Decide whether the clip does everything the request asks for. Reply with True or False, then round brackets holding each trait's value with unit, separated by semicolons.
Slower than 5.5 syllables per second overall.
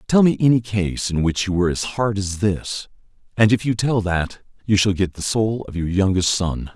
True (5.0 syllables/s)